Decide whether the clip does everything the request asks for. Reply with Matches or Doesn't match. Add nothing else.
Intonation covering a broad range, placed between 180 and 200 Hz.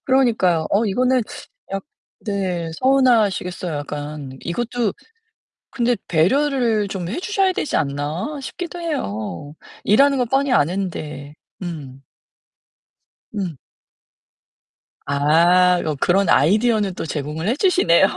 Matches